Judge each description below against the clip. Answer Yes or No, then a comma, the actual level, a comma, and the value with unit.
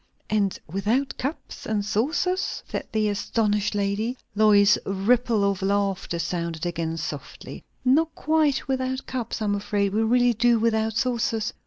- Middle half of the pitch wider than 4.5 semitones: No, average, 3.6 semitones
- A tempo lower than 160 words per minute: Yes, average, 145 wpm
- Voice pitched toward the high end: Yes, high, 215 Hz